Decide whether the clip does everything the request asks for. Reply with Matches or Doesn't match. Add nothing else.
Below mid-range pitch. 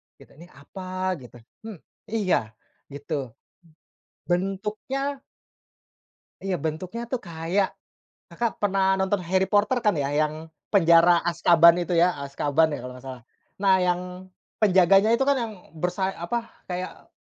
Doesn't match